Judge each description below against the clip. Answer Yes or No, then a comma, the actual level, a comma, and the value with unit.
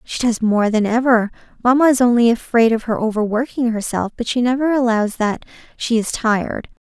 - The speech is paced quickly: No, average, 185 wpm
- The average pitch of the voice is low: No, high, 235 Hz